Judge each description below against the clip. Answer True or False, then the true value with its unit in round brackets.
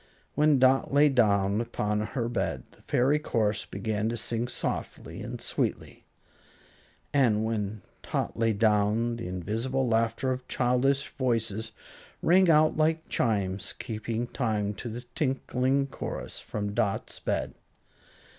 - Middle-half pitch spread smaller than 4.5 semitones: True (3.7 semitones)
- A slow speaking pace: True (130 wpm)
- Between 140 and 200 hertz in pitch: False (115 Hz)